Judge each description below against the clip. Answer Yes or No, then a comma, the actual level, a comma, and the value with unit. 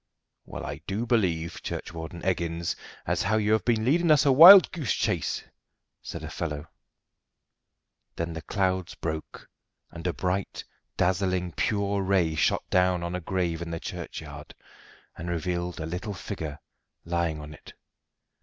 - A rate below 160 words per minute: Yes, average, 150 wpm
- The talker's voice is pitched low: Yes, very low, 90 Hz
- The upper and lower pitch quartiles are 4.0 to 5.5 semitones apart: No, average, 3.3 semitones